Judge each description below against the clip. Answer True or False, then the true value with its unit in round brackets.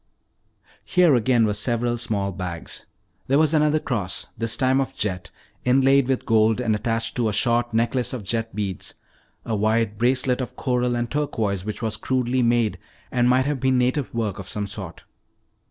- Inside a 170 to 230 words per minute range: True (175 wpm)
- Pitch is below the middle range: True (120 Hz)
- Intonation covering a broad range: False (3.2 semitones)